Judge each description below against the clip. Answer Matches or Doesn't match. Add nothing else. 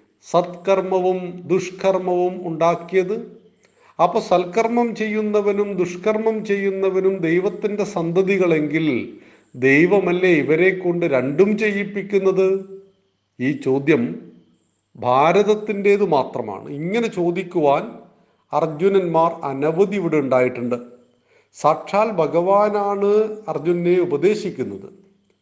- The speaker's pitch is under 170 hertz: Doesn't match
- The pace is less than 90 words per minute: Matches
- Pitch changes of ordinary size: Matches